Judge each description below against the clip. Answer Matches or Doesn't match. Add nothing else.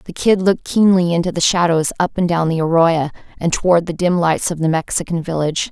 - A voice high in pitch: Doesn't match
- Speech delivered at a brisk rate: Matches